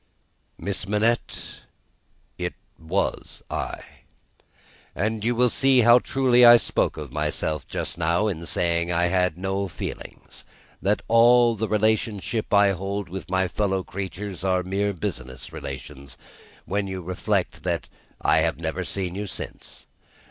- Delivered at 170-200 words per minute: No, average, 140 wpm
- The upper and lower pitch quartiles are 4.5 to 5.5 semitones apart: No, average, 3.6 semitones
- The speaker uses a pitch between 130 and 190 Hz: No, very low, 95 Hz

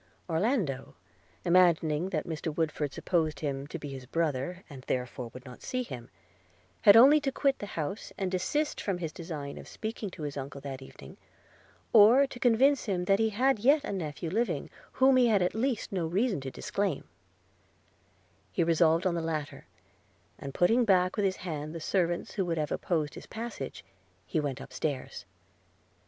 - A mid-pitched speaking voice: Yes, medium, 175 Hz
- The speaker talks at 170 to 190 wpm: Yes, average, 180 wpm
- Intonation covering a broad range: Yes, wide, 6.3 semitones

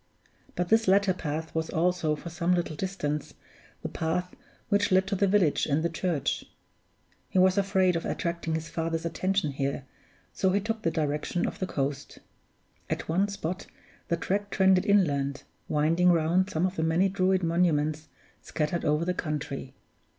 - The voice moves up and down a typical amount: Yes, average, 3.3 semitones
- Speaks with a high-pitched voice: No, medium, 170 Hz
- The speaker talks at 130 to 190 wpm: Yes, average, 165 wpm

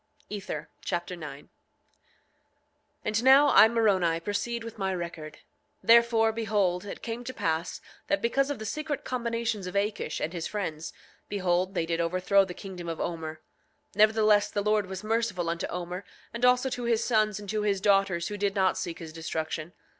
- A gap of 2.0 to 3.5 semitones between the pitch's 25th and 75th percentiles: No, average, 4.4 semitones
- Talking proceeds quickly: No, average, 180 wpm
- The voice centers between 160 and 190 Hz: No, high, 200 Hz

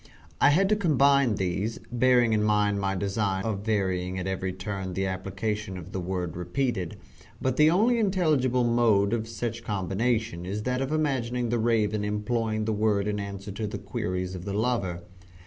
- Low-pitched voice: Yes, low, 105 Hz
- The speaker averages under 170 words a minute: No, average, 180 wpm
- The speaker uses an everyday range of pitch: Yes, average, 4.0 semitones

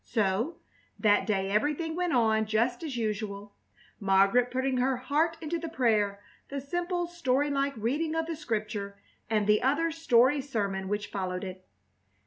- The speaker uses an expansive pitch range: Yes, wide, 6.3 semitones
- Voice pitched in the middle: No, high, 245 Hz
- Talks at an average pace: Yes, average, 150 wpm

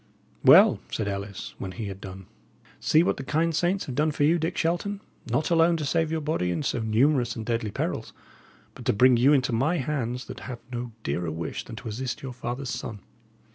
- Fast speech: Yes, fast, 215 wpm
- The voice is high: No, low, 125 Hz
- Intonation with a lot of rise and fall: Yes, wide, 5.8 semitones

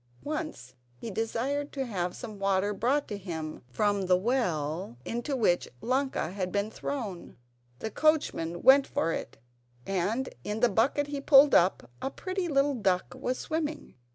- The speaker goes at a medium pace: Yes, average, 155 wpm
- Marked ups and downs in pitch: Yes, wide, 7.0 semitones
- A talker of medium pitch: No, high, 225 Hz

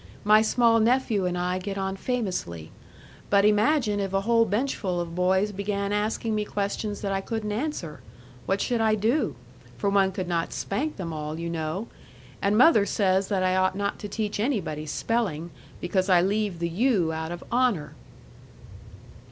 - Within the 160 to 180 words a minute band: Yes, average, 175 wpm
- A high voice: Yes, high, 200 Hz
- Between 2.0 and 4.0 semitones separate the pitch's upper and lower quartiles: Yes, average, 3.2 semitones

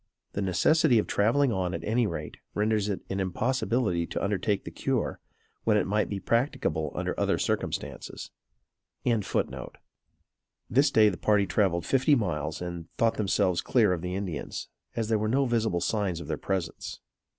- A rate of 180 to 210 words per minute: No, average, 160 wpm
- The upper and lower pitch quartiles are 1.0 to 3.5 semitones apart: No, average, 4.1 semitones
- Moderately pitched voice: No, low, 105 Hz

